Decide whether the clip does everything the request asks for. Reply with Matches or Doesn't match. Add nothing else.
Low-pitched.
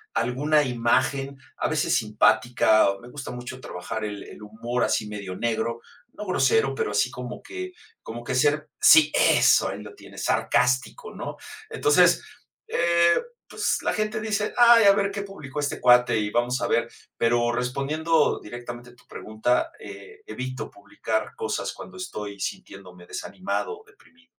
Matches